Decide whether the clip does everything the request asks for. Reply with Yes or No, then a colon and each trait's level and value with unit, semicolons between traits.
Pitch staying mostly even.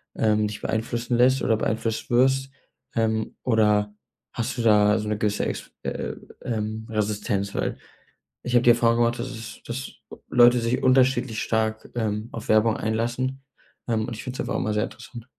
Yes: narrow, 2.0 semitones